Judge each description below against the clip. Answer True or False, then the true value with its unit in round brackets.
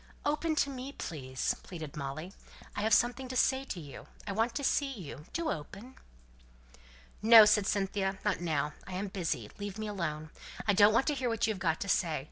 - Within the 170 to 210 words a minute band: True (205 wpm)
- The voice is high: True (205 Hz)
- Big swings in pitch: True (6.7 semitones)